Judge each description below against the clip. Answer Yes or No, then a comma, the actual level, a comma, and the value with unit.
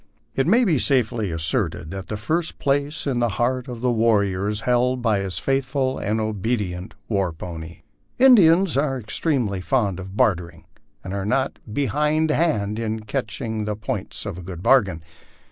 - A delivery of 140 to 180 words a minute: Yes, average, 165 wpm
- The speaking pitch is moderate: No, low, 110 Hz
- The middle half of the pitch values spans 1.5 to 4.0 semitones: No, wide, 5.4 semitones